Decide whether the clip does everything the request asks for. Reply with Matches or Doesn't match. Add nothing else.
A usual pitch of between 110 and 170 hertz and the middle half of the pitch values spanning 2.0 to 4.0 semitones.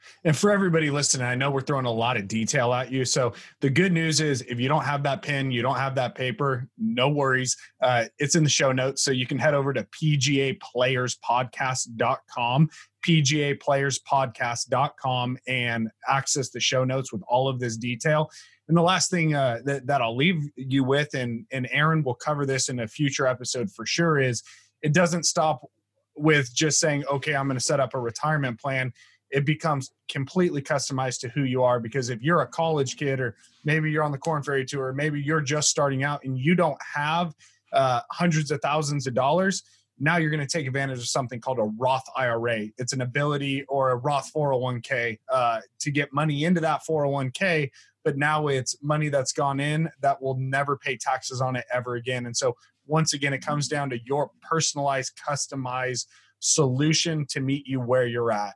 Matches